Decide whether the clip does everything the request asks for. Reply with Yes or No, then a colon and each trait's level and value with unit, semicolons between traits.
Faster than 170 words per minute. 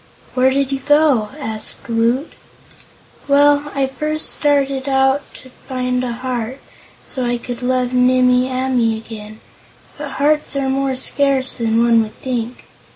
No: average, 145 wpm